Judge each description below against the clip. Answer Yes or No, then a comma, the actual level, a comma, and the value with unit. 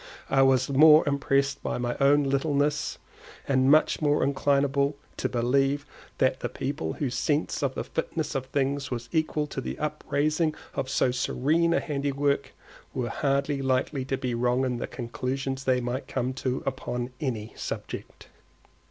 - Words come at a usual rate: Yes, average, 160 wpm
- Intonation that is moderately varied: No, narrow, 1.9 semitones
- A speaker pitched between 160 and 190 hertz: No, low, 135 Hz